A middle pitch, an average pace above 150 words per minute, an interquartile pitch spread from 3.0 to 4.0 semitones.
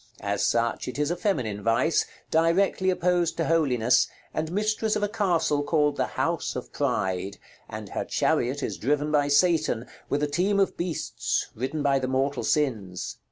No: medium, 150 Hz; average, 170 wpm; wide, 5.4 semitones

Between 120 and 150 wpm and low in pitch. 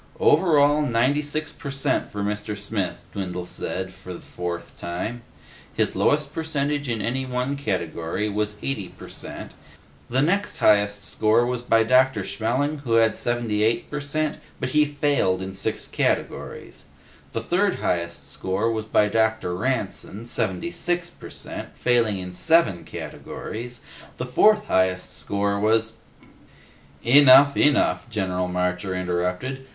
Yes: average, 145 wpm; low, 115 Hz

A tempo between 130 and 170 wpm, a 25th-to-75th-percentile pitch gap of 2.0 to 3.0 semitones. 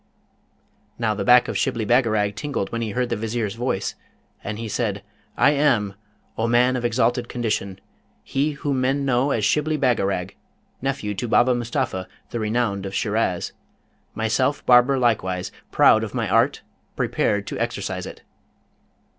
No: average, 155 wpm; average, 3.5 semitones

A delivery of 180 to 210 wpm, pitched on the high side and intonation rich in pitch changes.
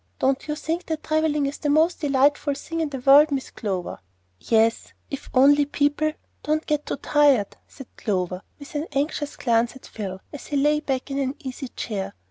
No: average, 190 wpm; very high, 280 Hz; average, 2.7 semitones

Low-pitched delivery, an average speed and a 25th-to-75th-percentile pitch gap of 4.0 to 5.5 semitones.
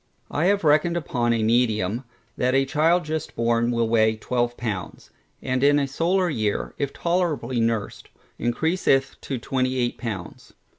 Yes: low, 130 Hz; average, 150 wpm; average, 4.6 semitones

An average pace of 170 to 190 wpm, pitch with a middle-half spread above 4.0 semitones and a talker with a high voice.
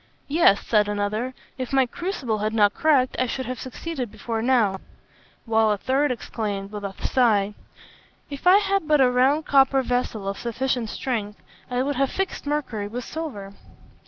Yes: average, 175 wpm; average, 4.4 semitones; very high, 250 Hz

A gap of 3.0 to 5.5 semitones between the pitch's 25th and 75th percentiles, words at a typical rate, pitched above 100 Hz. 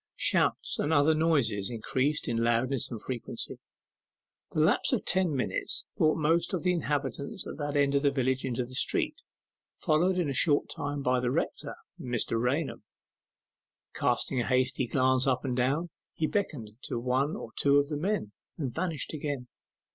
Yes: average, 3.6 semitones; average, 170 wpm; medium, 140 Hz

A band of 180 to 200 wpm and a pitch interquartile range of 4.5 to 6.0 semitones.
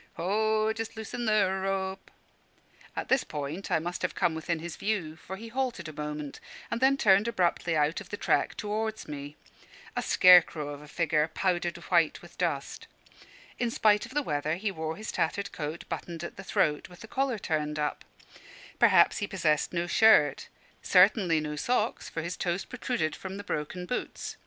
Yes: average, 185 wpm; wide, 5.4 semitones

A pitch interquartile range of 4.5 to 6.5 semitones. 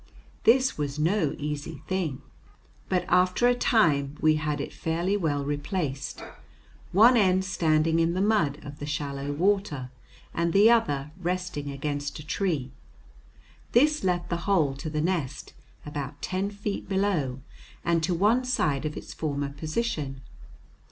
Yes: average, 4.8 semitones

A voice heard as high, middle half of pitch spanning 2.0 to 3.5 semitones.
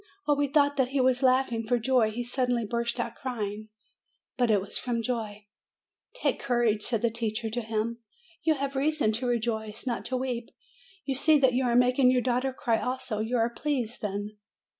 Yes: high, 240 Hz; narrow, 2.6 semitones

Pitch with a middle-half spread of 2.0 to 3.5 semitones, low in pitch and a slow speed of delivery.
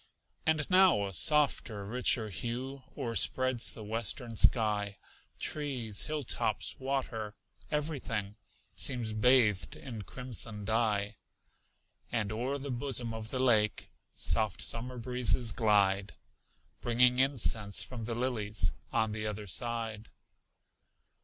Yes: average, 3.2 semitones; low, 115 Hz; slow, 110 wpm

